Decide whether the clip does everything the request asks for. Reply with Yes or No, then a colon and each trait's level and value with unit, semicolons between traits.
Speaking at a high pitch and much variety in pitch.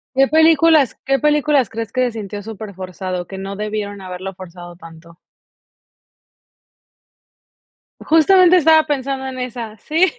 Yes: high, 225 Hz; wide, 7.7 semitones